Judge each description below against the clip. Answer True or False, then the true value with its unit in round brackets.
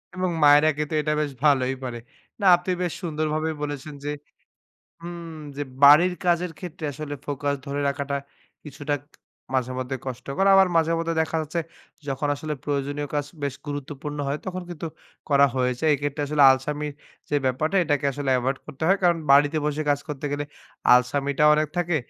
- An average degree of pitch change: False (2.0 semitones)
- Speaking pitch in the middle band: True (145 Hz)